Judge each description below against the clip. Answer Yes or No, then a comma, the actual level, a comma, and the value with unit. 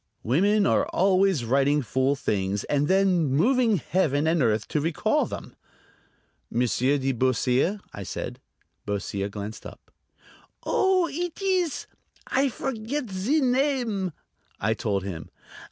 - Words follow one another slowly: Yes, slow, 125 wpm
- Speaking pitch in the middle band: Yes, medium, 160 Hz